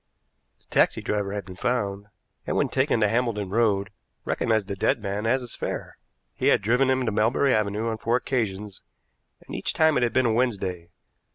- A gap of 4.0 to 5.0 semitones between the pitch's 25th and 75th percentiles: No, average, 3.5 semitones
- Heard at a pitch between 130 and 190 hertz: No, low, 110 Hz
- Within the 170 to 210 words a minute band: Yes, average, 195 wpm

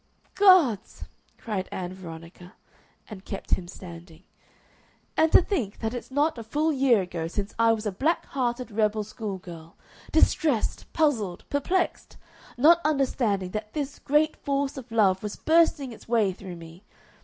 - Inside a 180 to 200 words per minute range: No, average, 155 wpm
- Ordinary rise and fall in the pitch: No, wide, 7.0 semitones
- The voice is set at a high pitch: Yes, high, 225 Hz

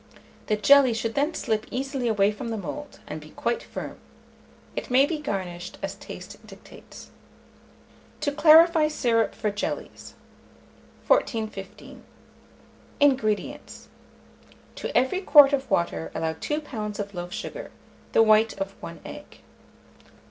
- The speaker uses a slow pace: Yes, slow, 130 wpm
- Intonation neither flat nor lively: No, wide, 5.9 semitones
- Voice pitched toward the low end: No, high, 230 Hz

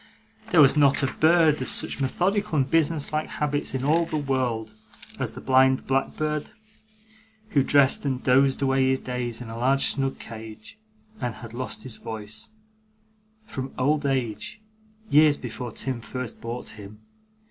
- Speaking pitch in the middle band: No, low, 130 Hz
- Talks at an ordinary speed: Yes, average, 160 wpm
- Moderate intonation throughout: Yes, average, 3.4 semitones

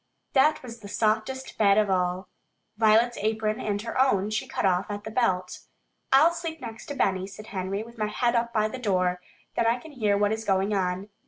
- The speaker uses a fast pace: Yes, fast, 215 wpm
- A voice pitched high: Yes, high, 215 Hz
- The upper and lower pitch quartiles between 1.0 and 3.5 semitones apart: Yes, average, 3.2 semitones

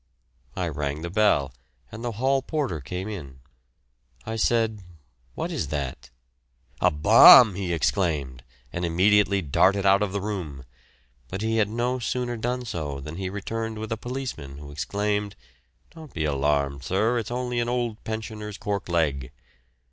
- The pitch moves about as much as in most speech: No, wide, 6.8 semitones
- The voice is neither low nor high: No, low, 100 Hz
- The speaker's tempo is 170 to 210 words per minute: No, average, 155 wpm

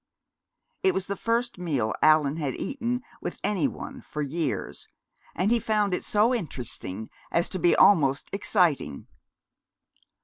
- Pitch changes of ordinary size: No, wide, 6.9 semitones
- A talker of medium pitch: Yes, medium, 180 Hz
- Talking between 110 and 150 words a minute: Yes, average, 140 wpm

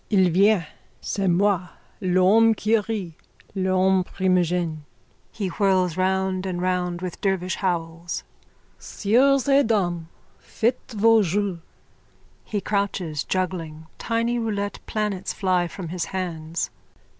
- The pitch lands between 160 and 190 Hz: Yes, medium, 185 Hz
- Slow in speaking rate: Yes, slow, 115 wpm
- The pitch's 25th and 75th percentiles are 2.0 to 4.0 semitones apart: Yes, average, 2.7 semitones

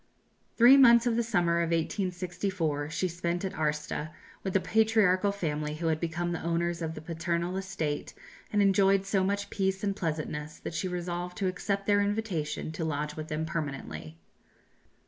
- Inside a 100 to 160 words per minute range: No, average, 170 wpm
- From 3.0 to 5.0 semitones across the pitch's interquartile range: Yes, average, 3.8 semitones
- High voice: No, medium, 175 Hz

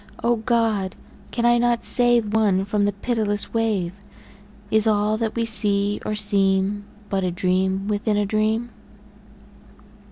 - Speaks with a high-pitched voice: Yes, high, 210 Hz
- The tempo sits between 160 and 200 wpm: No, average, 140 wpm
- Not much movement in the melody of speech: Yes, narrow, 2.1 semitones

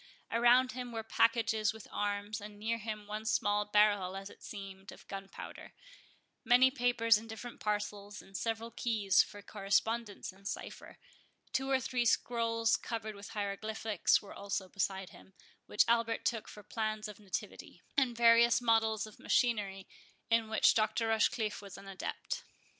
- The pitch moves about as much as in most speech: No, narrow, 2.2 semitones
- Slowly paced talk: No, average, 155 wpm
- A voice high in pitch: Yes, high, 215 Hz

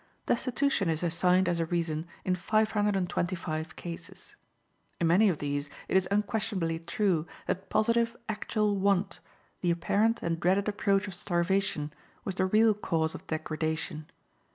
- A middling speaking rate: Yes, average, 155 wpm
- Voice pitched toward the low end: No, medium, 185 Hz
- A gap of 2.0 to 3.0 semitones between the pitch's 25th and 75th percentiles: No, average, 3.8 semitones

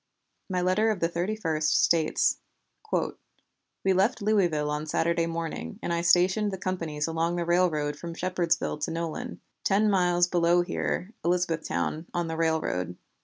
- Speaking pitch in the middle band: Yes, medium, 170 Hz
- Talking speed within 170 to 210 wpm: No, average, 145 wpm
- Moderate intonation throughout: No, narrow, 2.2 semitones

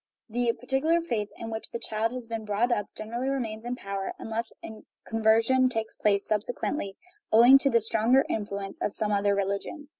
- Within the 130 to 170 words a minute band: No, average, 185 wpm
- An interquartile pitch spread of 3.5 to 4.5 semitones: No, average, 2.7 semitones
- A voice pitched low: No, high, 225 Hz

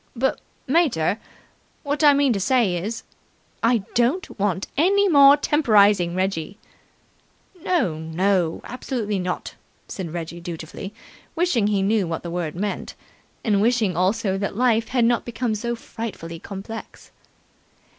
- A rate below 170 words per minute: Yes, slow, 135 wpm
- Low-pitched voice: No, high, 210 Hz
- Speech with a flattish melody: No, average, 5.2 semitones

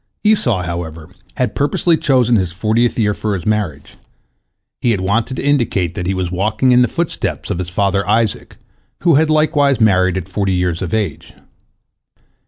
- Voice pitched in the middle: No, low, 105 Hz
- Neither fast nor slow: Yes, average, 175 wpm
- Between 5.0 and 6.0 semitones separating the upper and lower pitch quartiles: Yes, wide, 5.4 semitones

